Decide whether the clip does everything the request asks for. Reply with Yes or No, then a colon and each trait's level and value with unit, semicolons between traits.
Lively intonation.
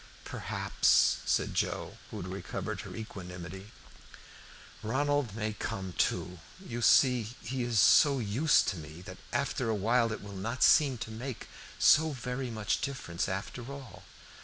No: average, 4.7 semitones